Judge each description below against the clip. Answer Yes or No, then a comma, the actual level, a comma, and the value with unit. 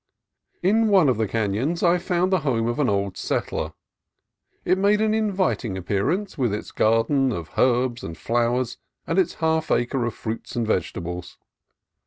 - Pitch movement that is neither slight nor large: No, wide, 8.3 semitones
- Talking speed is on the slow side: No, average, 165 wpm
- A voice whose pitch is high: No, low, 125 Hz